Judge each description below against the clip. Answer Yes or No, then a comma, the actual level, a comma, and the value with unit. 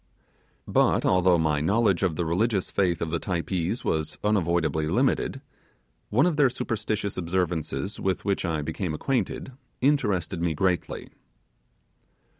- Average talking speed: No, slow, 130 wpm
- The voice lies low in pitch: Yes, very low, 90 Hz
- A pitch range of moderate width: Yes, average, 4.2 semitones